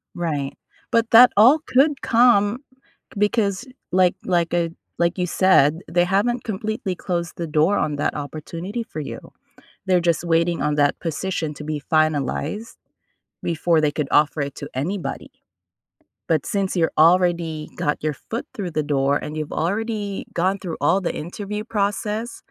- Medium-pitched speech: Yes, medium, 175 Hz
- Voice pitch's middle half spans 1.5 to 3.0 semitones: No, average, 4.8 semitones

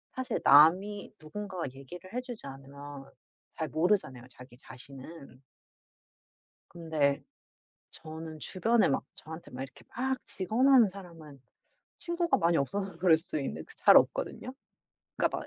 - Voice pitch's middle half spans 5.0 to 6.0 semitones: No, wide, 6.5 semitones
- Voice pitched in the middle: Yes, medium, 165 Hz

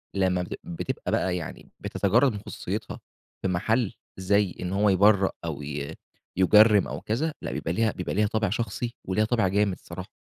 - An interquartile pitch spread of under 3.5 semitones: Yes, average, 3.0 semitones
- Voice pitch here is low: Yes, low, 100 Hz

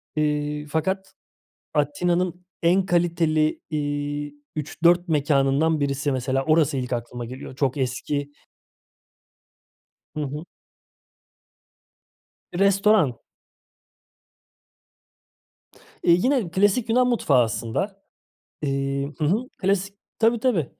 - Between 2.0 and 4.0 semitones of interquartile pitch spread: No, average, 4.8 semitones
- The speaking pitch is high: No, medium, 155 Hz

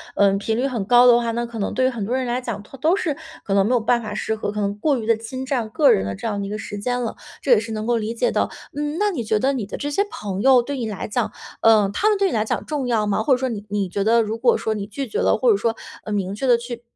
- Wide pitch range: No, average, 3.5 semitones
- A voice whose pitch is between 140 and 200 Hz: No, high, 230 Hz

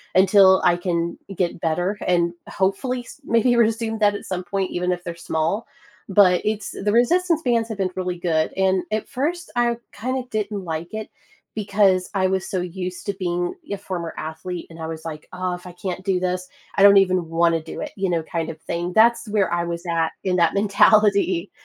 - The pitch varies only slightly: No, average, 3.3 semitones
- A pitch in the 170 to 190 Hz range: Yes, medium, 185 Hz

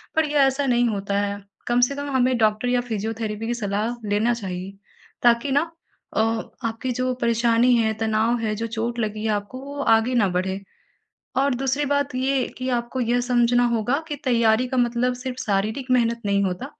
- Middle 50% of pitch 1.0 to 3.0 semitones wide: Yes, average, 2.7 semitones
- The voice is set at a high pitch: Yes, high, 235 Hz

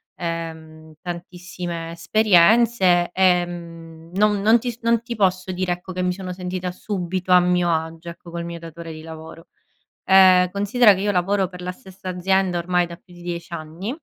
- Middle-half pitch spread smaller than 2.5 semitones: Yes, narrow, 2.1 semitones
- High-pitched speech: No, medium, 180 Hz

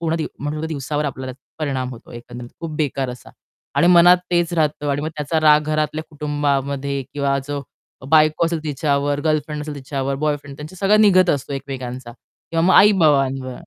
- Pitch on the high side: No, medium, 145 Hz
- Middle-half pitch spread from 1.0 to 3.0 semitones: Yes, narrow, 2.4 semitones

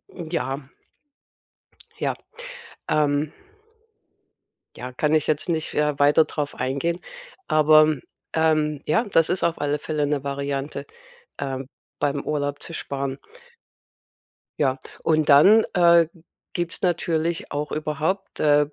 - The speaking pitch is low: No, medium, 150 Hz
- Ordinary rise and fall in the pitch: No, narrow, 2.1 semitones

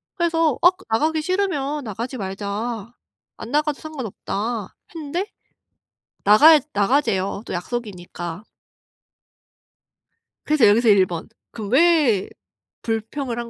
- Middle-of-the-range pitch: No, high, 235 Hz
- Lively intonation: Yes, wide, 6.8 semitones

